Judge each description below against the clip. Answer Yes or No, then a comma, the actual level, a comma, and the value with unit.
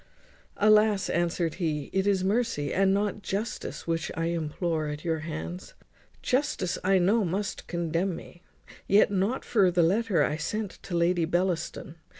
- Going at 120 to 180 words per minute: Yes, average, 155 wpm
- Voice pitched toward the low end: No, medium, 180 Hz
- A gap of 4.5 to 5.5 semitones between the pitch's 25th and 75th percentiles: No, average, 3.3 semitones